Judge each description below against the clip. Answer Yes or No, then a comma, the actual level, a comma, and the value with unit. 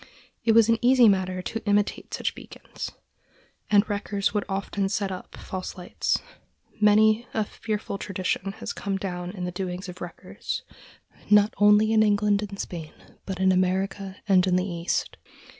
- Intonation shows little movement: Yes, narrow, 2.2 semitones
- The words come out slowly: No, average, 160 wpm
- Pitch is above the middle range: Yes, high, 200 Hz